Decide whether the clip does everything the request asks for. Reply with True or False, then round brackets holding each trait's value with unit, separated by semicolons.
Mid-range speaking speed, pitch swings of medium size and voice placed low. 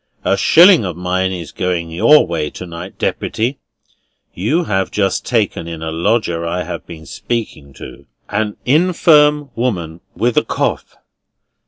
False (150 wpm; 6.5 semitones; 95 Hz)